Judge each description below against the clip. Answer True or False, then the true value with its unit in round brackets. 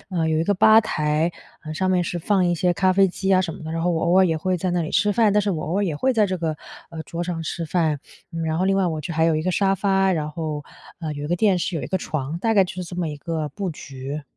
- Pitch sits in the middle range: True (175 Hz)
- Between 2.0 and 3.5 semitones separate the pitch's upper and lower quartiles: True (3.1 semitones)